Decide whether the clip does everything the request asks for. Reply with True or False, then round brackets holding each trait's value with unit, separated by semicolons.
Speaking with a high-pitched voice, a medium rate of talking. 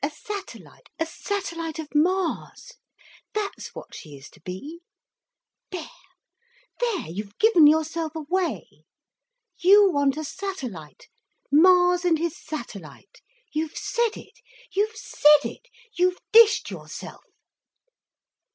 False (335 Hz; 95 wpm)